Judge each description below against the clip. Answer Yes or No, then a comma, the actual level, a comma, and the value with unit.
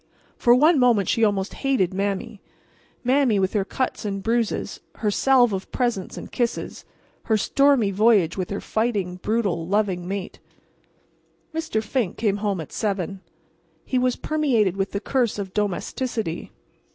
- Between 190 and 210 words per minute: No, average, 145 wpm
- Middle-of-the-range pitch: No, high, 210 Hz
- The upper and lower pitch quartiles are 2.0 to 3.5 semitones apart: No, average, 3.9 semitones